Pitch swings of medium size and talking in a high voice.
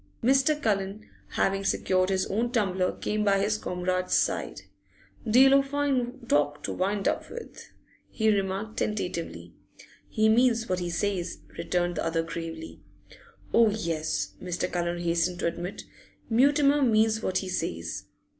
Yes: average, 4.5 semitones; high, 195 Hz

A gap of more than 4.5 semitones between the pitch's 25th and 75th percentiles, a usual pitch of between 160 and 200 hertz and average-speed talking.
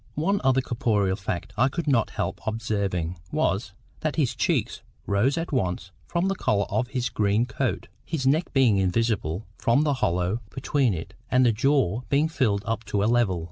No: average, 5.1 semitones; low, 115 Hz; average, 180 wpm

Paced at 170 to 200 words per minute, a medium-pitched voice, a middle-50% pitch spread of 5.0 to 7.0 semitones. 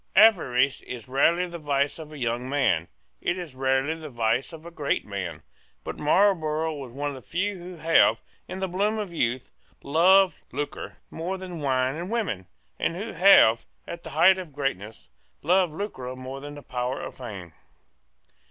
Yes: average, 175 wpm; medium, 150 Hz; wide, 5.6 semitones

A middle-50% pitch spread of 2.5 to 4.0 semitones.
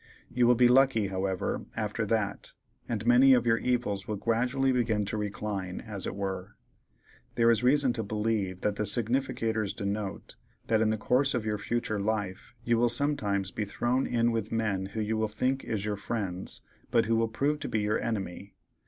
Yes: average, 2.8 semitones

